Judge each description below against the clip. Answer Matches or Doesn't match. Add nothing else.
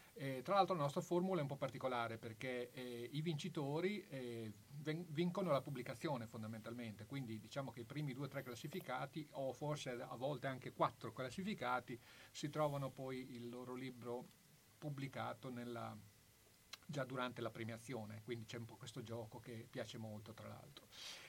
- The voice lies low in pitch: Matches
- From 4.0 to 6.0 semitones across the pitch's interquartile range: Doesn't match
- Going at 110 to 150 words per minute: Doesn't match